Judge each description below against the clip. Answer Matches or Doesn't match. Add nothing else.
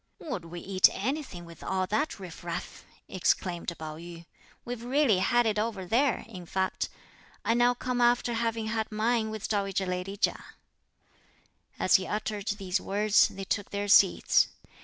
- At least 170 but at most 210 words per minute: Doesn't match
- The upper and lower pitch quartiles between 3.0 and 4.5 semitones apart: Matches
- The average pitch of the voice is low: Doesn't match